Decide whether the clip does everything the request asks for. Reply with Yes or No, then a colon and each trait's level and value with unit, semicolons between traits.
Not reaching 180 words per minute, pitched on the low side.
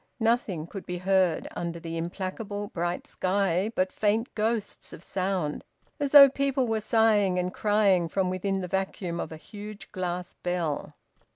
No: average, 160 wpm; high, 190 Hz